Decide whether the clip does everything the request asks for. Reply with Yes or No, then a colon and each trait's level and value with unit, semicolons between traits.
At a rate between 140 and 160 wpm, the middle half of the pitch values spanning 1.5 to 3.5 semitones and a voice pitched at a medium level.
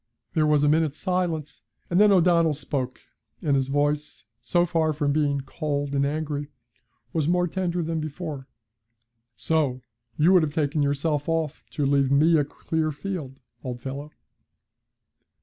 Yes: average, 150 wpm; narrow, 2.5 semitones; medium, 150 Hz